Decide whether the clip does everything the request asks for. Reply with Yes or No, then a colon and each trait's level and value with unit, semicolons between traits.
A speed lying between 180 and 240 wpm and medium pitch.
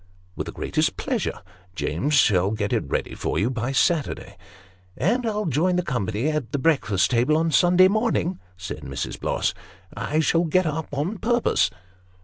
Yes: average, 185 wpm; medium, 150 Hz